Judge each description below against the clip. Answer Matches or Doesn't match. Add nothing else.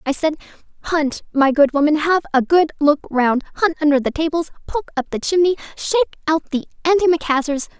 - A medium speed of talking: Matches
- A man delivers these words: Doesn't match